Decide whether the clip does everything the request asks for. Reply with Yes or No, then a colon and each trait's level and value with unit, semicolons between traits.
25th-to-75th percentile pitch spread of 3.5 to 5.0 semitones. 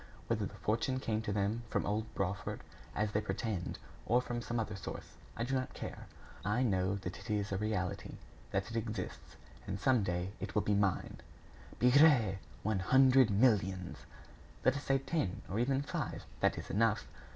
Yes: average, 3.9 semitones